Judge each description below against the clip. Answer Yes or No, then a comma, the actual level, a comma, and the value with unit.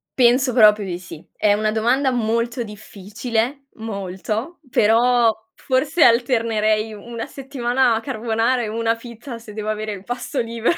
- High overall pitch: Yes, high, 230 Hz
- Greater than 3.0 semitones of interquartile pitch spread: No, narrow, 2.5 semitones